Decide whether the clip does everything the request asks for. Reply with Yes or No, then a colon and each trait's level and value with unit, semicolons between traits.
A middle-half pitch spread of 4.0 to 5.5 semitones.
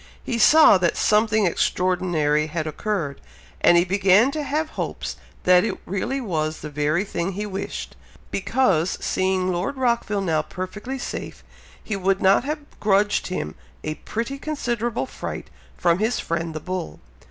Yes: average, 5.0 semitones